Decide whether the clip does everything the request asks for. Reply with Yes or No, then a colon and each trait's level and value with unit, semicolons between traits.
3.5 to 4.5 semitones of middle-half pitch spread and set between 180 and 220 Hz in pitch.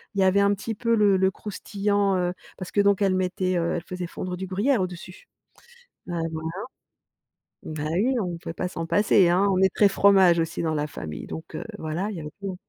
No: average, 2.8 semitones; medium, 185 Hz